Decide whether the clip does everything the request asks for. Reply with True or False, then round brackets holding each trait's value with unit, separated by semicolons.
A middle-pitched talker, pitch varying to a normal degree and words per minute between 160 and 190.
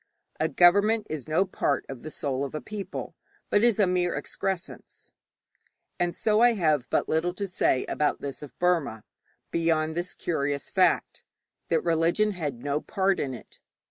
True (165 Hz; 4.5 semitones; 170 wpm)